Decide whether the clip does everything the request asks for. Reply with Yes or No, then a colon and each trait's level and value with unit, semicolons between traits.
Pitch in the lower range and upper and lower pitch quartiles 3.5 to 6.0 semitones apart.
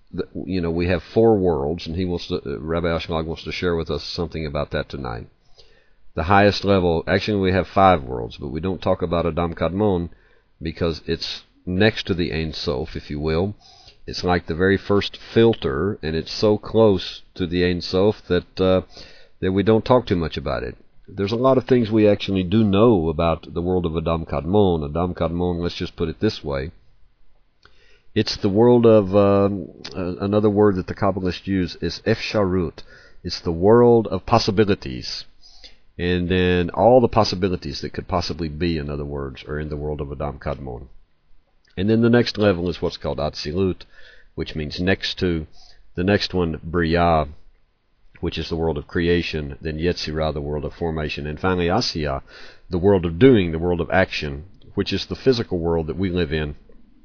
Yes: very low, 90 Hz; average, 3.8 semitones